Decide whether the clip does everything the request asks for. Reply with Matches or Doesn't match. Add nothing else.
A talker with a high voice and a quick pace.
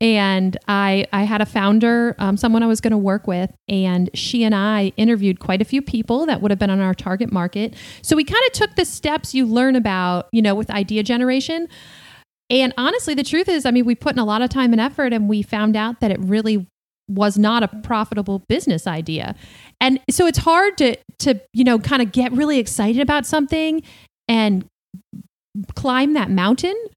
Matches